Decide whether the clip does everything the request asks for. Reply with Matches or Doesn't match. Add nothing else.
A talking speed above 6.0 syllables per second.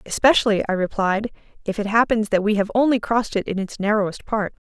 Matches